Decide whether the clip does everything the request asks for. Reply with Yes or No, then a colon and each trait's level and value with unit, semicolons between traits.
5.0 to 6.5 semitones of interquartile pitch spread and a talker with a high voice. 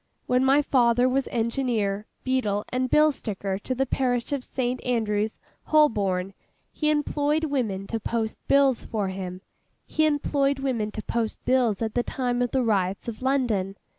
No: average, 4.2 semitones; high, 245 Hz